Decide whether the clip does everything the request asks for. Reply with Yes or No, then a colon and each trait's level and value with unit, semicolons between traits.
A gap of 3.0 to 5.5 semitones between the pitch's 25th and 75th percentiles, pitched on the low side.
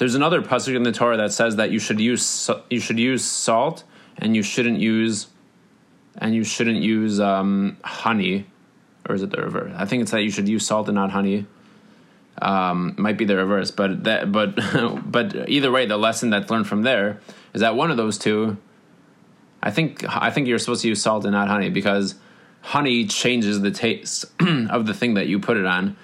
No: narrow, 2.5 semitones; low, 110 Hz